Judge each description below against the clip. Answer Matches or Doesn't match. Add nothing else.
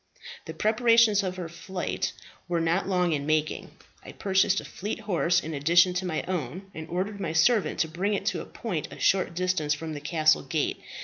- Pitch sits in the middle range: Matches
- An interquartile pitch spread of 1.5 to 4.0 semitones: Matches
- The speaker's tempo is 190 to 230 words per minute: Matches